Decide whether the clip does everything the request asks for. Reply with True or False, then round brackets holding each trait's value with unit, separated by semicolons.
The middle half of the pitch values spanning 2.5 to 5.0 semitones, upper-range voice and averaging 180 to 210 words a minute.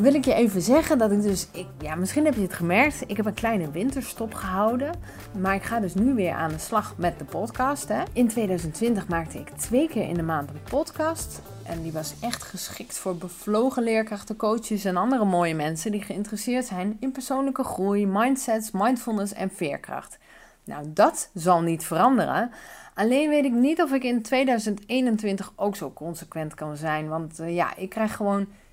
False (5.5 semitones; 210 Hz; 190 wpm)